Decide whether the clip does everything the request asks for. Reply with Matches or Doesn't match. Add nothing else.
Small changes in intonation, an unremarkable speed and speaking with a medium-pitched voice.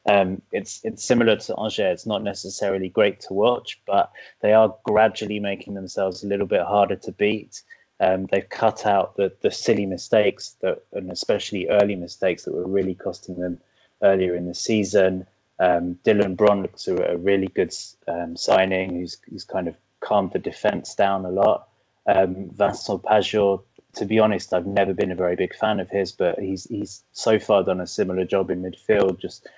Doesn't match